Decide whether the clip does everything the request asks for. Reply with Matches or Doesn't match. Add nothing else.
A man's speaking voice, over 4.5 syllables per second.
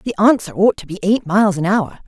Doesn't match